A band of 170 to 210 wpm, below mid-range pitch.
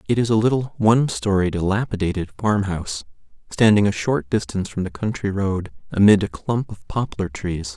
Yes: average, 180 wpm; low, 105 Hz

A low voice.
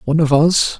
No: medium, 155 Hz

